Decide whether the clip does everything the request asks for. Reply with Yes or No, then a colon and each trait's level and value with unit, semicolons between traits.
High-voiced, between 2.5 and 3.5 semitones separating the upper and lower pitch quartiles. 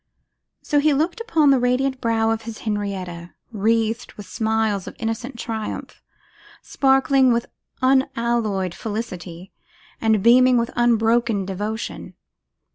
Yes: high, 225 Hz; average, 3.1 semitones